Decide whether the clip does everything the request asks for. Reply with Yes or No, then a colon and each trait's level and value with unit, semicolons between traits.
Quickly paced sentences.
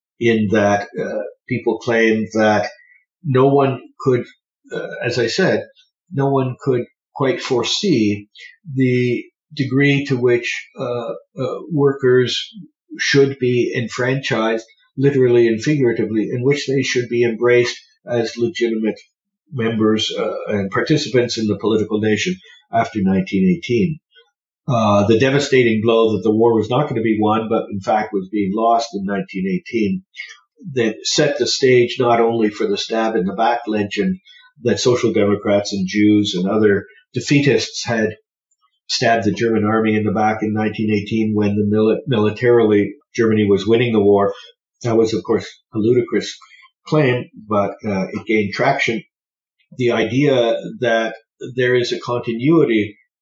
No: average, 145 wpm